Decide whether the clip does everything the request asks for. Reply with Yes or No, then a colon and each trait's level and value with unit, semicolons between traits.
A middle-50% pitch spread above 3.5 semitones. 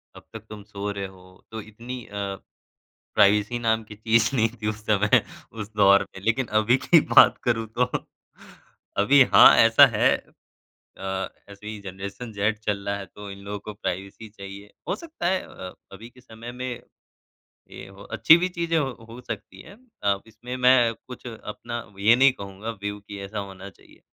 No: average, 3.2 semitones